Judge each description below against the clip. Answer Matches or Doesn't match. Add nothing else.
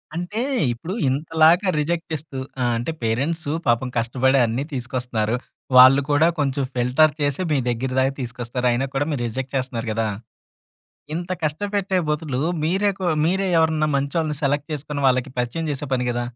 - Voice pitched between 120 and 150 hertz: Matches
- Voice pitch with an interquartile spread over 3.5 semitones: Matches